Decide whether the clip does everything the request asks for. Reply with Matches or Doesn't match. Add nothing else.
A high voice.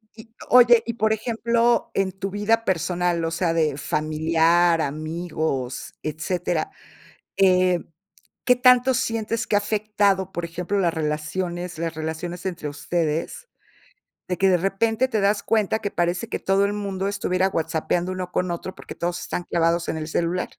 Doesn't match